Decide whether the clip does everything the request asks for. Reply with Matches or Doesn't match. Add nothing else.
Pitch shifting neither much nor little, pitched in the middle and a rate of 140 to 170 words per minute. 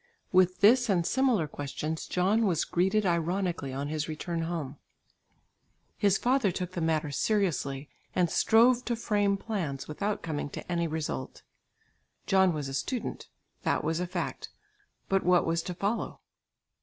Matches